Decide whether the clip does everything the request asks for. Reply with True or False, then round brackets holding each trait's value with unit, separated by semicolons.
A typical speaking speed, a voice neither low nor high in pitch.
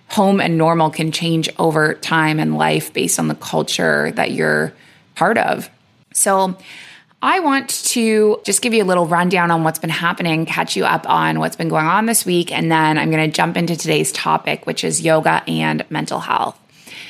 True (195 wpm; 165 Hz)